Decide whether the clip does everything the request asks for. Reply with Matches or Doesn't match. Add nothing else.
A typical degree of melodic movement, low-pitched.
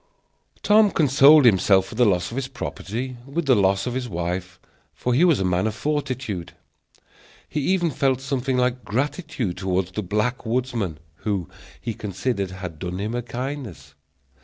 Doesn't match